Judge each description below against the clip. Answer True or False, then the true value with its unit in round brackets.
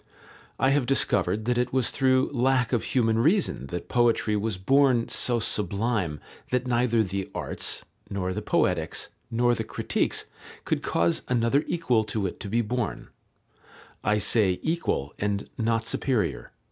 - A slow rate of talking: False (150 wpm)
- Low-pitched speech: True (115 Hz)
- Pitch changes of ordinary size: True (3.9 semitones)